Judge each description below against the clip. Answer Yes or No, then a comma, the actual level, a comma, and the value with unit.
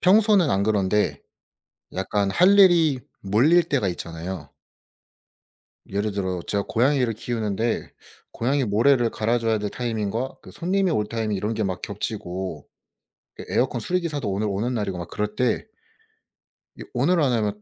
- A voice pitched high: No, low, 110 Hz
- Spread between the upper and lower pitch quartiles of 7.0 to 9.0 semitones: No, average, 5.2 semitones